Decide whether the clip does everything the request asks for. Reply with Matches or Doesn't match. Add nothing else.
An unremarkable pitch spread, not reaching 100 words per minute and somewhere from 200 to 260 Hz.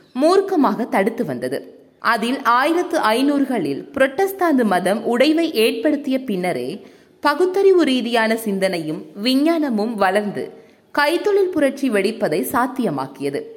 Doesn't match